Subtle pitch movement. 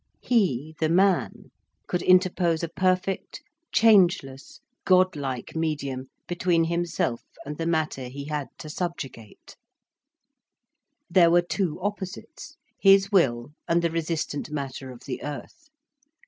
No: average, 4.5 semitones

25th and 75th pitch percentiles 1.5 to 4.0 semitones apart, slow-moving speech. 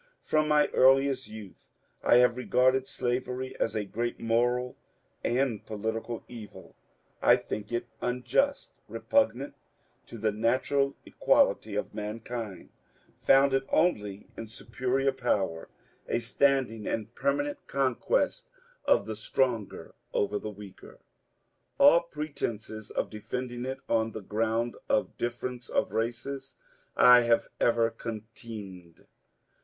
Yes: average, 3.3 semitones; slow, 115 wpm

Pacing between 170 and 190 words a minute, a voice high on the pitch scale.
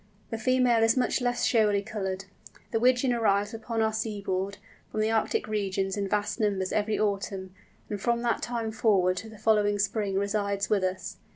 Yes: average, 180 wpm; high, 210 Hz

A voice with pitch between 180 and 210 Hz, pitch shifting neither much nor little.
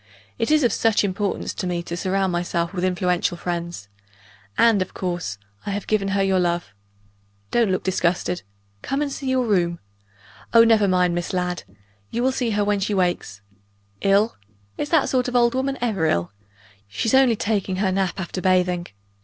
Yes: high, 190 Hz; average, 4.2 semitones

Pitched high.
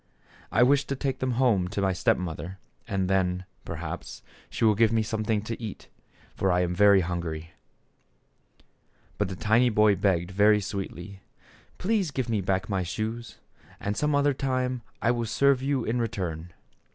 No: low, 105 Hz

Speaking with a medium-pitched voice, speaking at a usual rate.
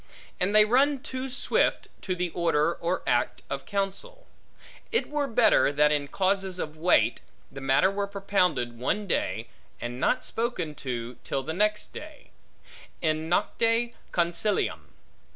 Yes: medium, 180 Hz; average, 145 wpm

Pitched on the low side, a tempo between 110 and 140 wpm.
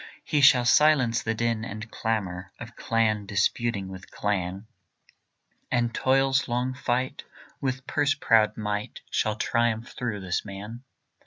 Yes: low, 115 Hz; slow, 135 wpm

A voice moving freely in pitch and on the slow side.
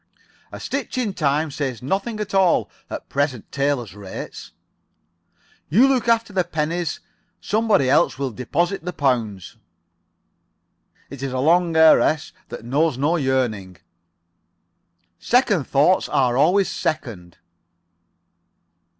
Yes: wide, 6.0 semitones; slow, 115 wpm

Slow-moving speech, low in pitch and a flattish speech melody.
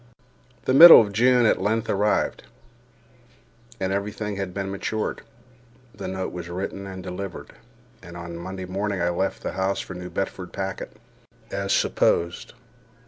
No: average, 160 wpm; very low, 95 Hz; narrow, 2.1 semitones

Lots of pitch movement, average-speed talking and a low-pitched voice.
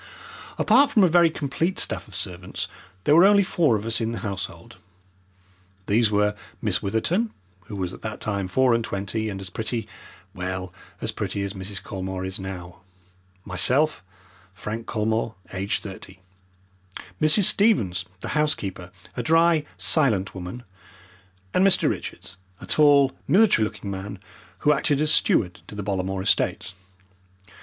Yes: wide, 7.7 semitones; average, 150 wpm; low, 105 Hz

